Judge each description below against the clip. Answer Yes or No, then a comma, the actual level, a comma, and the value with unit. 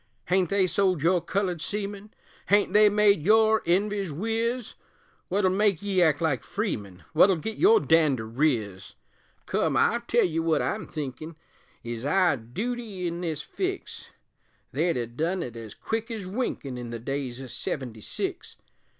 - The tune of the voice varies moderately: No, wide, 6.8 semitones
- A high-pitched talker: No, medium, 180 Hz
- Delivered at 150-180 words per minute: Yes, average, 160 wpm